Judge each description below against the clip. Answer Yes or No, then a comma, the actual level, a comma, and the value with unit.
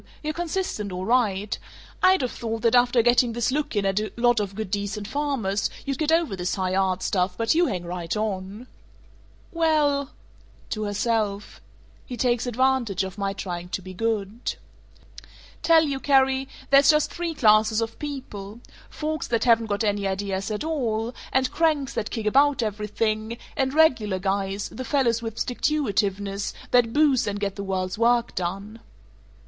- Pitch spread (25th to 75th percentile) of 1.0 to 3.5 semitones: No, average, 4.9 semitones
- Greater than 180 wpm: No, average, 170 wpm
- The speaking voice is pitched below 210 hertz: No, high, 225 Hz